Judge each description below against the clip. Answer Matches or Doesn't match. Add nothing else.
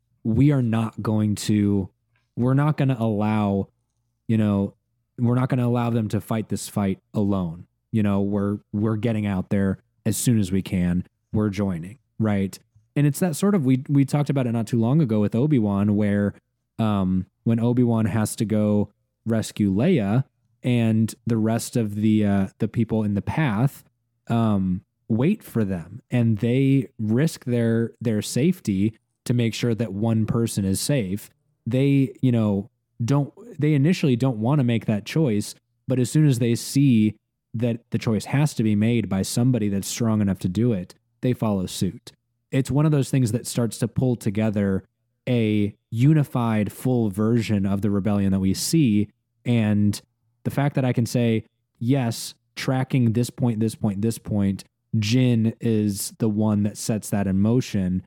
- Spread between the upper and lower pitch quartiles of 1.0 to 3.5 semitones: Matches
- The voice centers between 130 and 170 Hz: Doesn't match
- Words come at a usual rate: Matches